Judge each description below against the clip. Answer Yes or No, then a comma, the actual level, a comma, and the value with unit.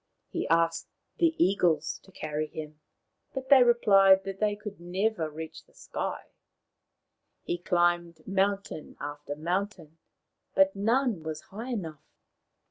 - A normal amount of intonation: Yes, average, 4.7 semitones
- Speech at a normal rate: No, slow, 125 wpm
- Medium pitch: Yes, medium, 180 Hz